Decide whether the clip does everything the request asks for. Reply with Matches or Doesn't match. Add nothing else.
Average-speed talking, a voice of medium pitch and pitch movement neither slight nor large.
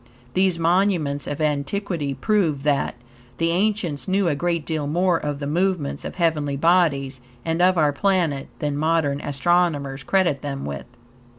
Matches